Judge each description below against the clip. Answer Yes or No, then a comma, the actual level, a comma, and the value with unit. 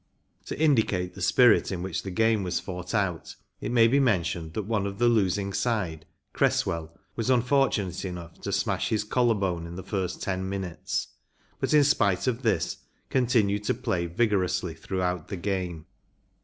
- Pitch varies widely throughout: No, average, 4.1 semitones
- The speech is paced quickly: No, average, 170 wpm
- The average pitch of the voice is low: Yes, low, 100 Hz